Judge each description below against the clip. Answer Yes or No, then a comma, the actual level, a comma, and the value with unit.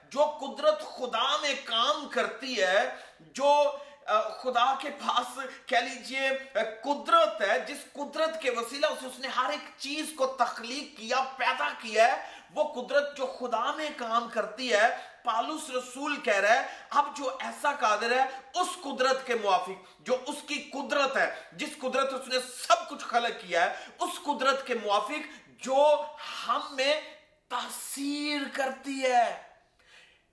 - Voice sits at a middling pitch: No, very high, 270 Hz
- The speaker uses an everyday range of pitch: Yes, average, 3.1 semitones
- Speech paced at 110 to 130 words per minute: No, average, 150 wpm